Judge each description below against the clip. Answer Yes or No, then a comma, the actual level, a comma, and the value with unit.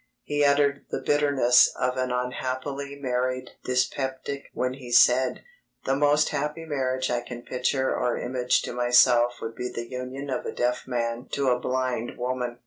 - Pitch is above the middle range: No, low, 130 Hz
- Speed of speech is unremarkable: Yes, average, 165 wpm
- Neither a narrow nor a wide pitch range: No, narrow, 1.9 semitones